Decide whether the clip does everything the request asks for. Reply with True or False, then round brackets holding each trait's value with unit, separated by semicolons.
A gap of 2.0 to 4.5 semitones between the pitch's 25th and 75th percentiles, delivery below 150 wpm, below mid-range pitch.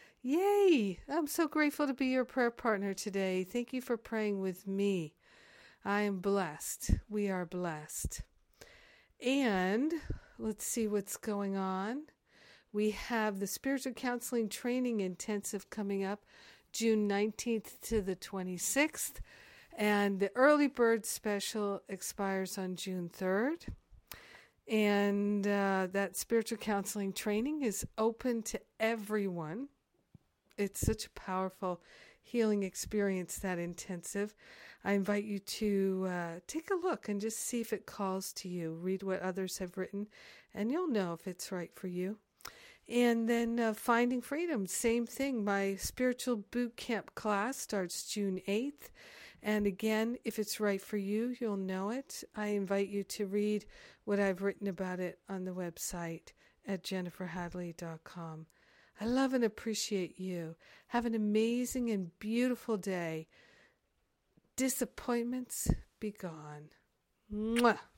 False (3.6 semitones; 135 wpm; 205 Hz)